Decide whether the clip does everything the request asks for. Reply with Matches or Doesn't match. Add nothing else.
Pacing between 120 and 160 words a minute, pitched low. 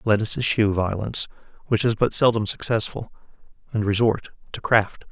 Matches